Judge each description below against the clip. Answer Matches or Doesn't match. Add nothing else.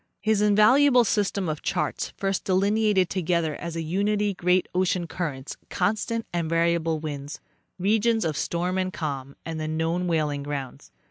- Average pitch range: Matches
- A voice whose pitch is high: Doesn't match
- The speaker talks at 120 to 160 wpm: Matches